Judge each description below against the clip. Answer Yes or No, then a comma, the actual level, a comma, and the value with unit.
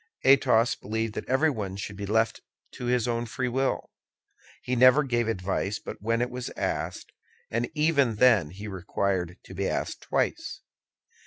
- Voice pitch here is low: Yes, low, 115 Hz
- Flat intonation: No, average, 4.0 semitones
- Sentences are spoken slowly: No, average, 160 wpm